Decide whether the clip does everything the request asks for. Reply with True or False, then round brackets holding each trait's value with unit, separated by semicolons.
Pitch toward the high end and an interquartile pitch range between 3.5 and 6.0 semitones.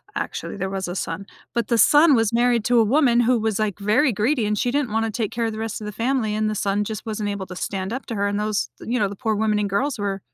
False (215 Hz; 2.7 semitones)